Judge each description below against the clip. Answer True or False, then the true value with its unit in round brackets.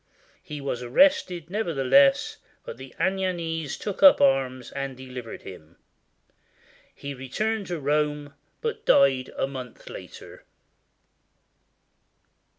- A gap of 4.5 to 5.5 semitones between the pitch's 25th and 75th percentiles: True (5.0 semitones)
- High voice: False (140 Hz)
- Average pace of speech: False (105 wpm)